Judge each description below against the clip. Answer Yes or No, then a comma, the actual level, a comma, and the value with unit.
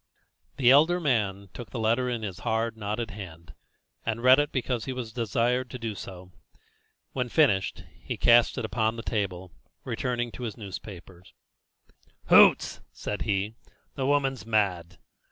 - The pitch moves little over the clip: No, average, 4.0 semitones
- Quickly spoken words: No, average, 155 wpm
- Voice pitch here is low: Yes, low, 115 Hz